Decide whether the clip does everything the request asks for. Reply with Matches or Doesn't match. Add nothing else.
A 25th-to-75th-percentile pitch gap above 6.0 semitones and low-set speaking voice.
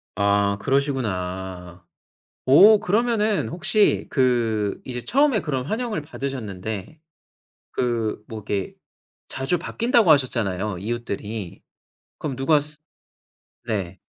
Matches